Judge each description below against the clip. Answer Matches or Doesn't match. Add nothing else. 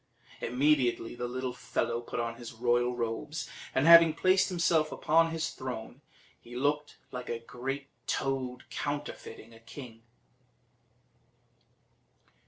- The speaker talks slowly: Matches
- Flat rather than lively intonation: Doesn't match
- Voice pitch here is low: Matches